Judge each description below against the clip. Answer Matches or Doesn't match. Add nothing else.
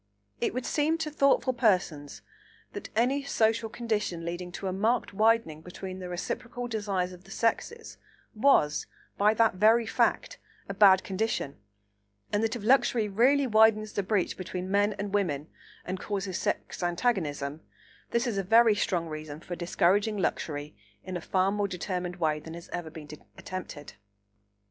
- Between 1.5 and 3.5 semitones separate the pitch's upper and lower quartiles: Doesn't match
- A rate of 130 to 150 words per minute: Doesn't match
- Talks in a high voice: Matches